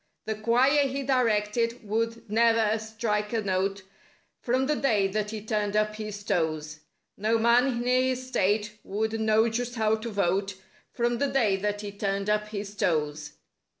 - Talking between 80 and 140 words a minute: No, average, 165 wpm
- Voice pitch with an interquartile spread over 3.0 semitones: No, narrow, 2.4 semitones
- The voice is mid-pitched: No, high, 215 Hz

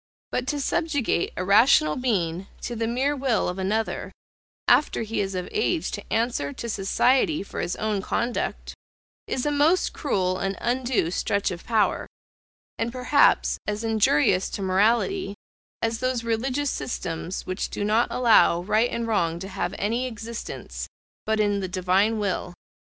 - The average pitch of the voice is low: No, high, 220 Hz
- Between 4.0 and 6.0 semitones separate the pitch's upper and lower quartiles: Yes, average, 4.6 semitones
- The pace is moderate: Yes, average, 155 wpm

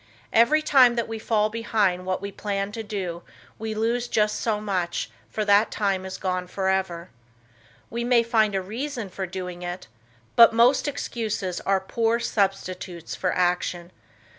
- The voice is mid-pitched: No, high, 205 Hz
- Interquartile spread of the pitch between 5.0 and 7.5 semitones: No, average, 3.6 semitones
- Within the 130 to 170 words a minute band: Yes, average, 160 wpm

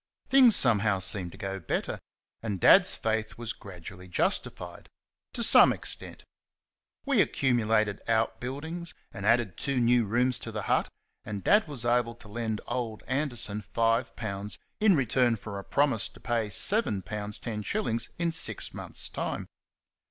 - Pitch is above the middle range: No, low, 115 Hz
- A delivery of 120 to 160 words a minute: Yes, average, 155 wpm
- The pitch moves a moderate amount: Yes, average, 3.6 semitones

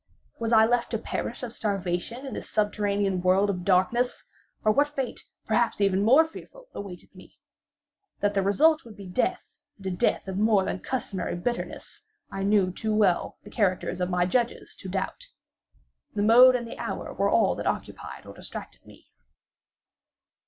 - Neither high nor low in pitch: No, high, 205 Hz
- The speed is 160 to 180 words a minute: Yes, average, 175 wpm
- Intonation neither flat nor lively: Yes, average, 3.9 semitones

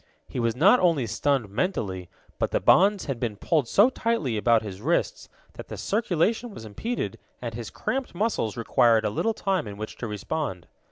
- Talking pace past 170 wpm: Yes, average, 185 wpm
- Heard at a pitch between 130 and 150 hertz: Yes, low, 135 Hz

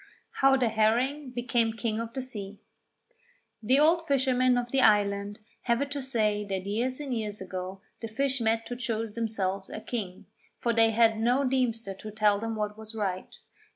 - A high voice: Yes, high, 225 Hz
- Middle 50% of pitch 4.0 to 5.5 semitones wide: No, average, 3.2 semitones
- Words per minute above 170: Yes, average, 185 wpm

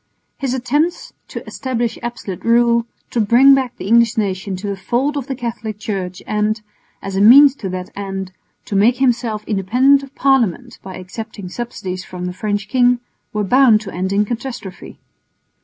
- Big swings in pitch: No, average, 4.1 semitones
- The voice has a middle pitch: No, high, 225 Hz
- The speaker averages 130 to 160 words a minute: No, average, 175 wpm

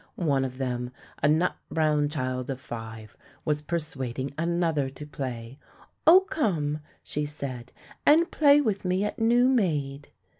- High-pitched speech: No, medium, 150 Hz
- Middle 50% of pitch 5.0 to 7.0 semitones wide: Yes, wide, 5.5 semitones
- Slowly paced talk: No, average, 145 wpm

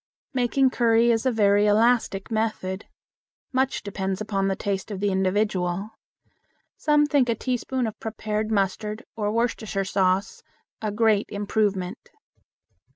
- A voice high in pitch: Yes, high, 215 Hz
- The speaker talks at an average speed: No, slow, 130 wpm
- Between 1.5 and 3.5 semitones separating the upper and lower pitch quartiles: Yes, average, 2.8 semitones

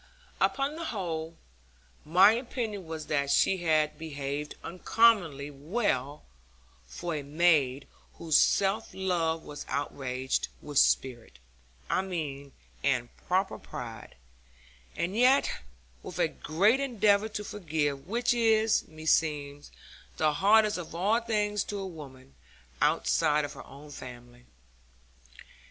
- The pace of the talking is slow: Yes, slow, 120 wpm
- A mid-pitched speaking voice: Yes, medium, 160 Hz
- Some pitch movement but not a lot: No, wide, 6.4 semitones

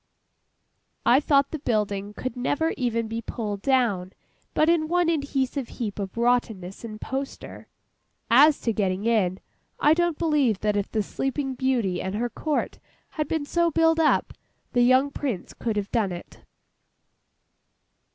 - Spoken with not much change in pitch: No, wide, 5.6 semitones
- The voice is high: Yes, high, 245 Hz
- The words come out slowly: No, average, 150 wpm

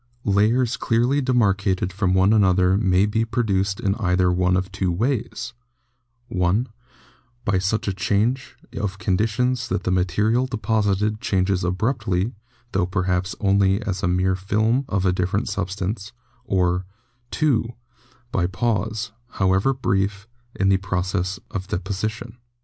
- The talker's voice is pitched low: Yes, low, 100 Hz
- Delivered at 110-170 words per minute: Yes, average, 140 wpm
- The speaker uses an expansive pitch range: No, average, 2.9 semitones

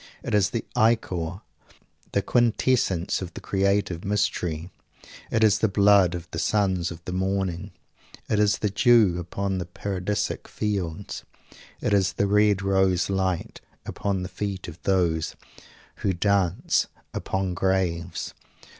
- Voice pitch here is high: No, very low, 95 Hz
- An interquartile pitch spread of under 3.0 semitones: Yes, narrow, 2.4 semitones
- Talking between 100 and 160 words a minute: Yes, slow, 135 wpm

